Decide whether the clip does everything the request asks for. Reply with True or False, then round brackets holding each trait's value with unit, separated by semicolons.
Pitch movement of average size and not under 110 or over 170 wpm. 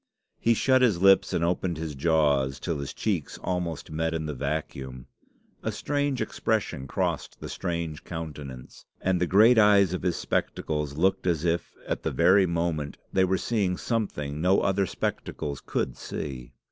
True (4.3 semitones; 165 wpm)